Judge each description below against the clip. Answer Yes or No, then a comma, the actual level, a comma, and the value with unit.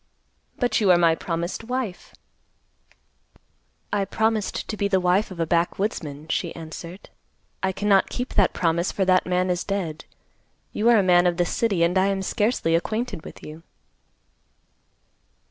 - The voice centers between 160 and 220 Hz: Yes, medium, 185 Hz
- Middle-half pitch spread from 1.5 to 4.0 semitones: Yes, average, 3.4 semitones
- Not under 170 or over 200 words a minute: No, average, 160 wpm